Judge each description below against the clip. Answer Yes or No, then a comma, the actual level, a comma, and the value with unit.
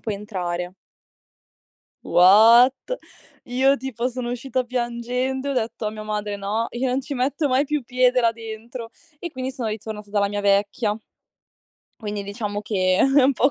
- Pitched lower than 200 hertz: No, high, 230 Hz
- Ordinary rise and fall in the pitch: Yes, average, 3.5 semitones